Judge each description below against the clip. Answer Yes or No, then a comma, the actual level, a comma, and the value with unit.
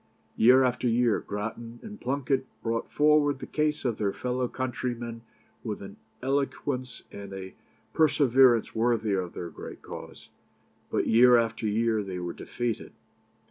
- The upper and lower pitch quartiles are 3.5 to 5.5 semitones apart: No, average, 3.0 semitones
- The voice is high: No, low, 120 Hz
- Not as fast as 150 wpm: Yes, average, 140 wpm